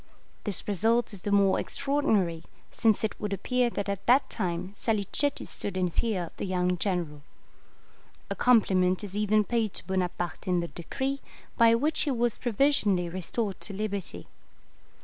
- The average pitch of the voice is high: Yes, high, 200 Hz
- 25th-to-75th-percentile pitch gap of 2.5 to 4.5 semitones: Yes, average, 4.2 semitones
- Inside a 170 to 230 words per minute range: No, average, 160 wpm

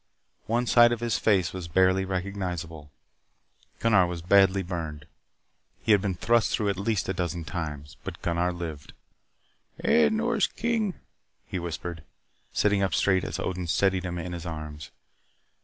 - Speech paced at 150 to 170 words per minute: Yes, average, 155 wpm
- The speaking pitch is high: No, very low, 90 Hz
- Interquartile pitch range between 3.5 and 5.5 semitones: No, average, 3.0 semitones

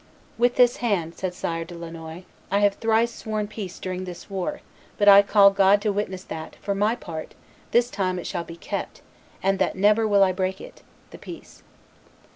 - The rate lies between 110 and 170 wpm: No, average, 195 wpm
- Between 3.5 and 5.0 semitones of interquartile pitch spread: No, average, 2.7 semitones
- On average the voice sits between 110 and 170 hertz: No, high, 195 Hz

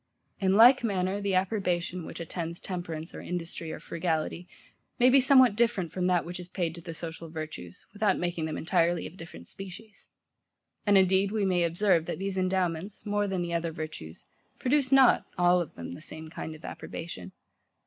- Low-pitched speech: No, medium, 180 Hz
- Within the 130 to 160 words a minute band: No, average, 190 wpm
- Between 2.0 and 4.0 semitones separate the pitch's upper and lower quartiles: Yes, average, 3.2 semitones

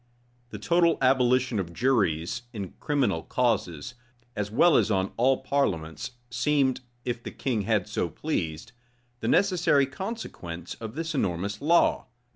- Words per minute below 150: Yes, slow, 135 wpm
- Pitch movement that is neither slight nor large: No, wide, 6.7 semitones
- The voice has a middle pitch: No, low, 120 Hz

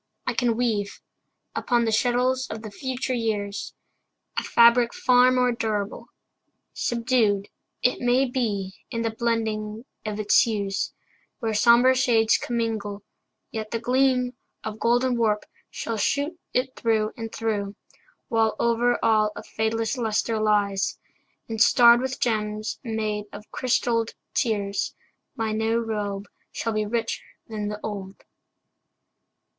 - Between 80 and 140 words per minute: Yes, slow, 135 wpm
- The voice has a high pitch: Yes, high, 225 Hz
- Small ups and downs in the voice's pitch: Yes, narrow, 2.2 semitones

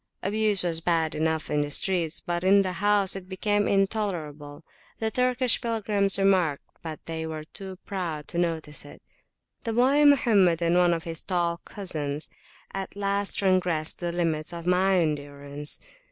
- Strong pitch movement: No, average, 3.8 semitones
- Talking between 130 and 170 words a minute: Yes, average, 160 wpm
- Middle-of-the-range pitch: Yes, medium, 175 Hz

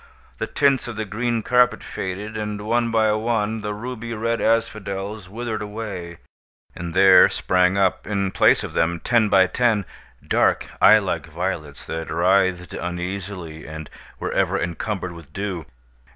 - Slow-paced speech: No, average, 150 wpm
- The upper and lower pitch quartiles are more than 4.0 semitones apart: No, average, 3.7 semitones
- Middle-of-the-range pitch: No, low, 100 Hz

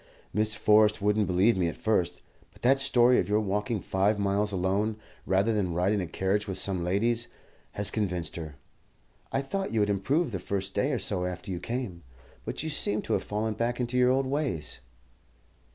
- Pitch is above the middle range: No, low, 105 Hz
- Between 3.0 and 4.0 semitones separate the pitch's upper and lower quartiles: Yes, average, 3.7 semitones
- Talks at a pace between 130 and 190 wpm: No, average, 200 wpm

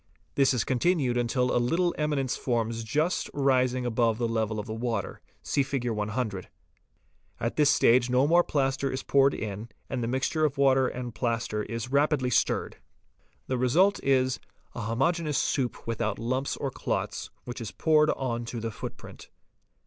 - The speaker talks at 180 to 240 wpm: No, average, 165 wpm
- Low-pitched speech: Yes, low, 125 Hz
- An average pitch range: Yes, average, 3.1 semitones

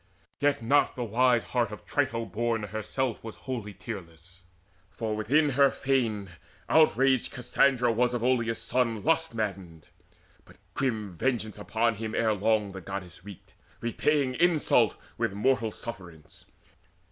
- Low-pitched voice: Yes, low, 115 Hz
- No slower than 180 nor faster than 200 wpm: No, slow, 135 wpm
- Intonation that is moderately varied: Yes, average, 3.8 semitones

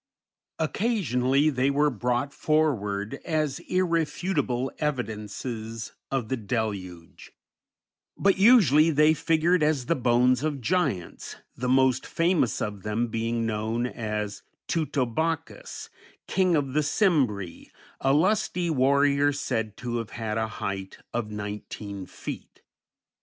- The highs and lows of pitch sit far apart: Yes, wide, 5.7 semitones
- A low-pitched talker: Yes, low, 130 Hz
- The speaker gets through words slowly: Yes, slow, 115 wpm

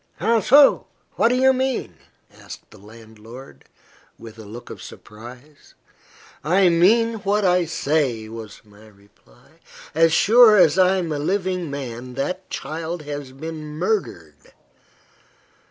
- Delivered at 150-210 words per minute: No, slow, 135 wpm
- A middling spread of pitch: No, wide, 8.5 semitones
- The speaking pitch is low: No, medium, 155 Hz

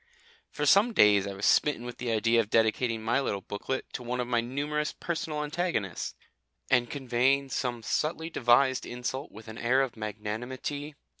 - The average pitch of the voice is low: Yes, low, 125 Hz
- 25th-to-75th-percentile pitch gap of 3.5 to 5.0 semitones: Yes, average, 3.9 semitones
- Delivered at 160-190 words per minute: Yes, average, 170 wpm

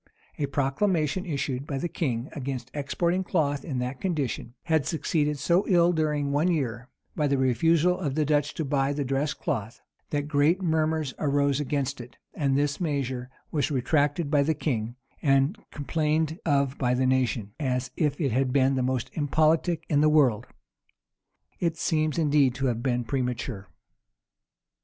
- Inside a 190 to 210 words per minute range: No, average, 165 wpm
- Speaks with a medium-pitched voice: Yes, medium, 145 Hz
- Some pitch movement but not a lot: Yes, average, 3.0 semitones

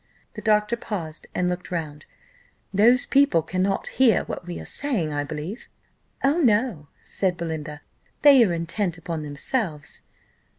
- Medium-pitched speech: Yes, medium, 180 Hz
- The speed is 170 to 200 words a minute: No, average, 140 wpm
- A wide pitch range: Yes, wide, 6.3 semitones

